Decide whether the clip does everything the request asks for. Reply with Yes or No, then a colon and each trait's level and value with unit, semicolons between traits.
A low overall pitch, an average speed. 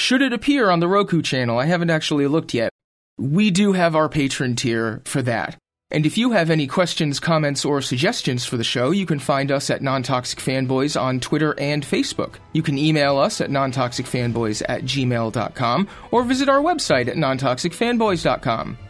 No: medium, 150 Hz; average, 180 wpm